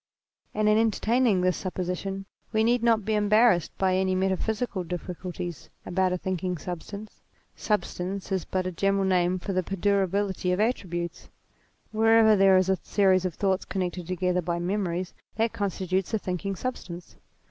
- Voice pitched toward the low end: No, high, 190 Hz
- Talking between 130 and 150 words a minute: No, average, 160 wpm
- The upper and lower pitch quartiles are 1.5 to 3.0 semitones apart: Yes, narrow, 2.4 semitones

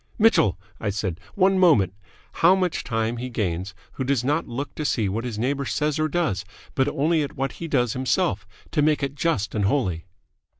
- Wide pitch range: Yes, wide, 6.3 semitones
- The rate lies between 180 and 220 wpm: Yes, average, 200 wpm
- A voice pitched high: No, low, 130 Hz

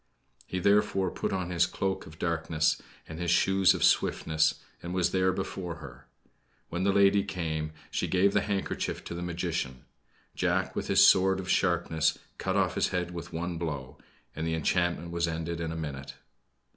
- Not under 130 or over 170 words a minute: No, average, 180 wpm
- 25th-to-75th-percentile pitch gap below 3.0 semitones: Yes, narrow, 2.6 semitones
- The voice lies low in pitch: Yes, very low, 85 Hz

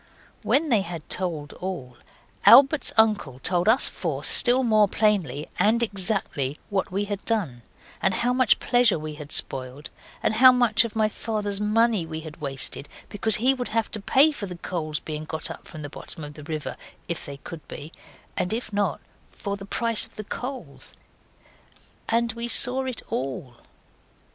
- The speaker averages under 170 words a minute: No, average, 175 wpm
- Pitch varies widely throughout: Yes, wide, 6.8 semitones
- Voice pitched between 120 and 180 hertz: No, high, 200 Hz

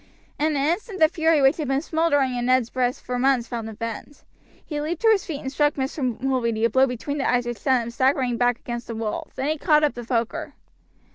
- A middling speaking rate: No, fast, 240 wpm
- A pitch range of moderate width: Yes, average, 3.7 semitones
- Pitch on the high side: Yes, very high, 265 Hz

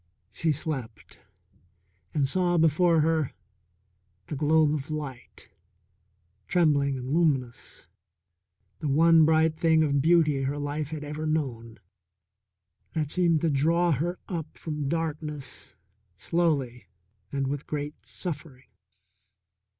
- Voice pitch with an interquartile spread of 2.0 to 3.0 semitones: Yes, narrow, 2.6 semitones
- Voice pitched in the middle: Yes, medium, 150 Hz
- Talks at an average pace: No, slow, 110 wpm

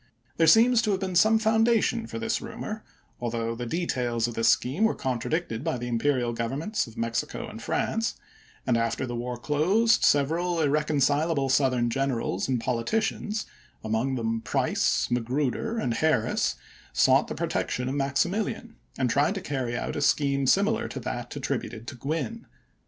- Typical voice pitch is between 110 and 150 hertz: Yes, medium, 140 Hz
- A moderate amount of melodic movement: No, wide, 7.8 semitones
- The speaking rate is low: No, average, 165 wpm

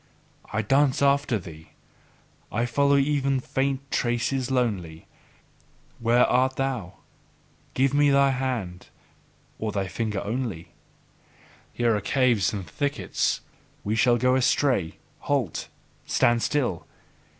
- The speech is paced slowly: Yes, slow, 115 wpm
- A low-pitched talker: Yes, low, 125 Hz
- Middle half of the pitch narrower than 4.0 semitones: No, average, 4.3 semitones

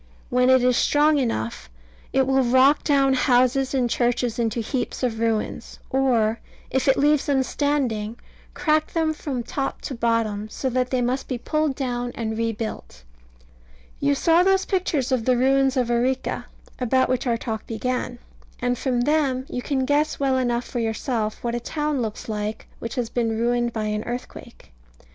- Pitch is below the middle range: No, very high, 250 Hz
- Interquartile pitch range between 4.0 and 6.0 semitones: No, average, 2.7 semitones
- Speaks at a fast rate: No, average, 175 wpm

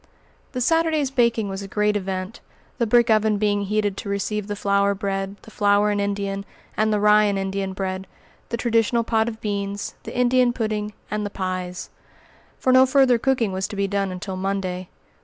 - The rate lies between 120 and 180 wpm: No, average, 190 wpm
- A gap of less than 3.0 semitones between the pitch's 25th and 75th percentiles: Yes, narrow, 2.4 semitones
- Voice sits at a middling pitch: No, high, 205 Hz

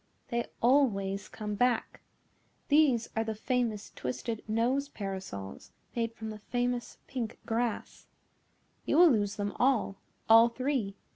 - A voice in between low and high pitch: No, high, 230 Hz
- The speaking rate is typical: No, slow, 130 wpm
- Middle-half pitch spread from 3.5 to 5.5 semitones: No, average, 3.1 semitones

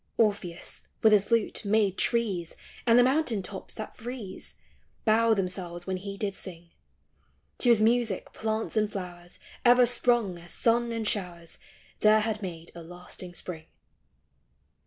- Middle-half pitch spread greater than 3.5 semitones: Yes, average, 4.1 semitones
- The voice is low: No, high, 205 Hz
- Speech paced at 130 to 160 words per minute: Yes, average, 150 wpm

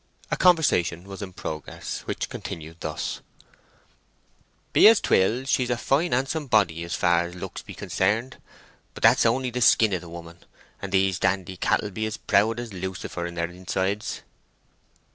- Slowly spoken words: No, average, 165 wpm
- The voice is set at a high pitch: No, very low, 95 Hz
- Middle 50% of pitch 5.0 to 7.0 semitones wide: Yes, wide, 5.4 semitones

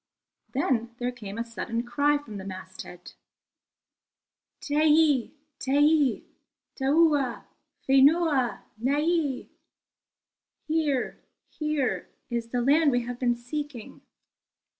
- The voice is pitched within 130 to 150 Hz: No, very high, 265 Hz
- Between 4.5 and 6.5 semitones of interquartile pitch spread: No, average, 3.8 semitones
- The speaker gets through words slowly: Yes, slow, 95 wpm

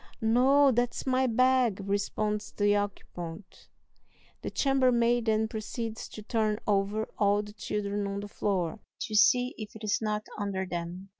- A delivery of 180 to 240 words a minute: No, average, 150 wpm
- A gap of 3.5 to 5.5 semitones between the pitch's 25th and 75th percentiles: No, average, 2.7 semitones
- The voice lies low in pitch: No, high, 215 Hz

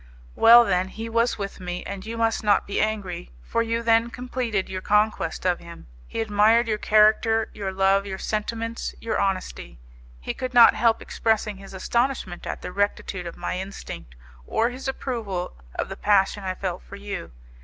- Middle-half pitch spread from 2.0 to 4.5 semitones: Yes, average, 3.1 semitones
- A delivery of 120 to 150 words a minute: No, average, 180 wpm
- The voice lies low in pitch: No, high, 210 Hz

